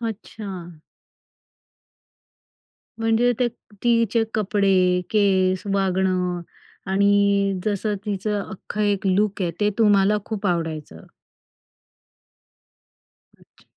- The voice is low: No, high, 200 Hz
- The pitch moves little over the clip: Yes, narrow, 2.2 semitones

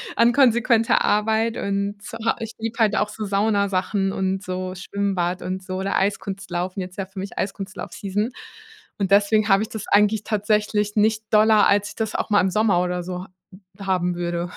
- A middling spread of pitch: No, narrow, 2.3 semitones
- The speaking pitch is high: Yes, high, 200 Hz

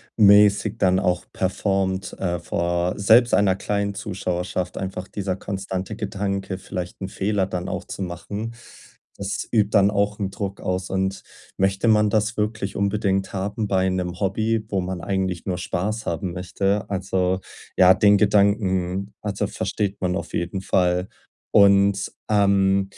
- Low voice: Yes, very low, 95 Hz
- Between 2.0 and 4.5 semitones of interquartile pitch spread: No, narrow, 1.6 semitones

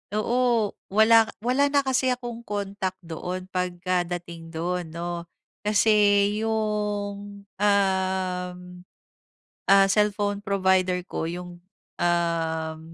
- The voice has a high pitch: Yes, high, 195 Hz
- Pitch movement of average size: Yes, average, 3.0 semitones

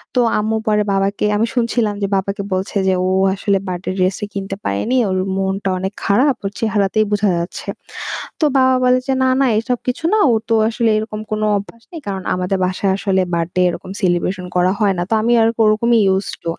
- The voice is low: No, high, 200 Hz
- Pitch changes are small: No, average, 3.1 semitones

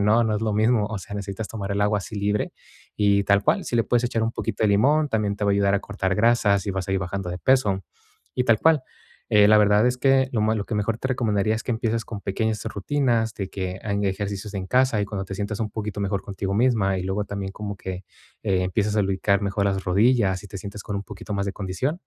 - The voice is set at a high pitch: No, low, 105 Hz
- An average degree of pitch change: No, narrow, 2.2 semitones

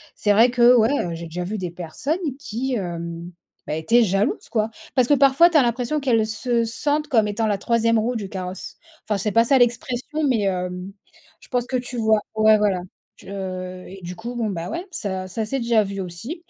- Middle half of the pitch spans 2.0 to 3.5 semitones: No, average, 4.5 semitones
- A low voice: No, high, 220 Hz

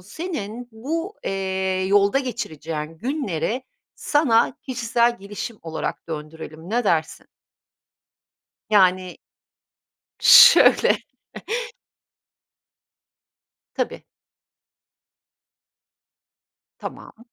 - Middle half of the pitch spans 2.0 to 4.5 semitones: No, wide, 5.4 semitones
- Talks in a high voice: Yes, high, 205 Hz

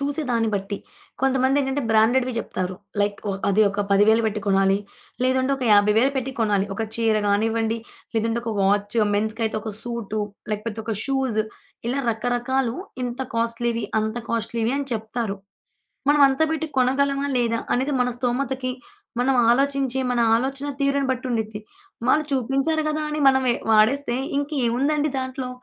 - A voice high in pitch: Yes, high, 240 Hz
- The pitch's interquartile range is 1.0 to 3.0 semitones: No, average, 3.5 semitones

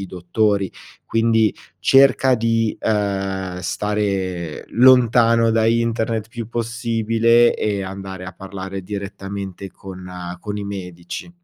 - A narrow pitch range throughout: No, average, 3.0 semitones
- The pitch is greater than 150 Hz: No, low, 105 Hz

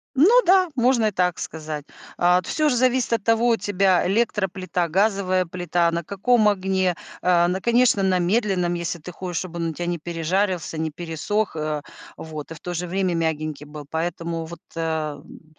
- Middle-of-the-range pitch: Yes, medium, 180 Hz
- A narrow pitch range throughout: No, average, 3.6 semitones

